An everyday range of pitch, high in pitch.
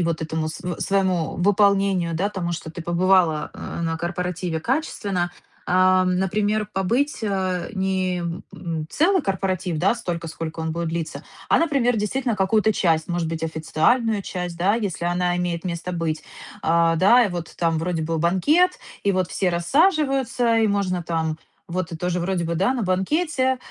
No: average, 3.4 semitones; medium, 180 Hz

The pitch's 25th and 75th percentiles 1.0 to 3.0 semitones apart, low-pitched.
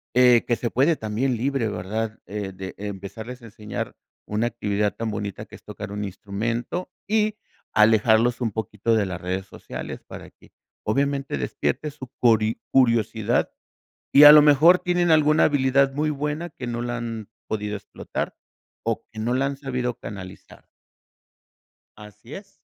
No: average, 4.6 semitones; low, 115 Hz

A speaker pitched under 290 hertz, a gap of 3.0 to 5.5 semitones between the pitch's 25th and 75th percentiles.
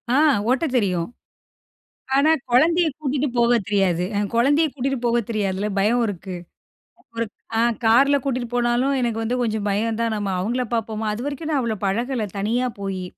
Yes: high, 235 Hz; average, 4.0 semitones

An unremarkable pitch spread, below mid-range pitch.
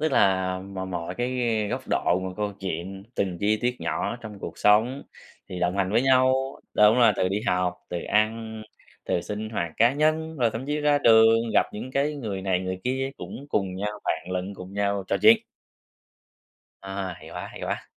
Yes: average, 4.8 semitones; low, 105 Hz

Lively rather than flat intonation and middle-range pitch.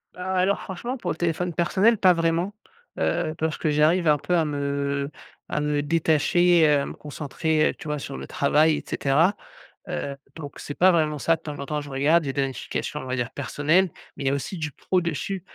No: average, 3.3 semitones; medium, 155 Hz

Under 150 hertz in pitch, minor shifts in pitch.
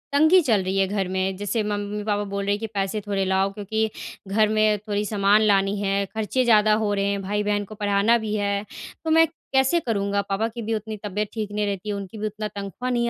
No: high, 205 Hz; narrow, 1.5 semitones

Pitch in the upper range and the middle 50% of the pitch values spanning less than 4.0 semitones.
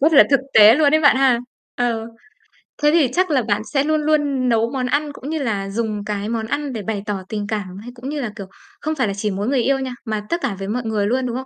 No: high, 245 Hz; average, 5.0 semitones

